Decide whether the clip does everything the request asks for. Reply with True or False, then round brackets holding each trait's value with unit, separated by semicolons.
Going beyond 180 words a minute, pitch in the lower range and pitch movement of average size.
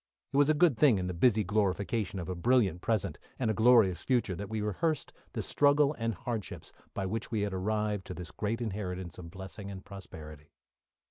True (200 wpm; 105 Hz; 3.8 semitones)